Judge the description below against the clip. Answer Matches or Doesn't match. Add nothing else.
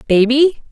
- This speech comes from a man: Doesn't match